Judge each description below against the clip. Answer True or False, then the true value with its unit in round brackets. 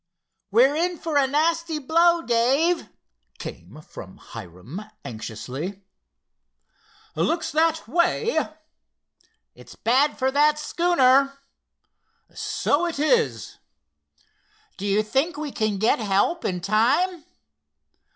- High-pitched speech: True (275 Hz)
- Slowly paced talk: True (100 wpm)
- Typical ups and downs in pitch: False (8.3 semitones)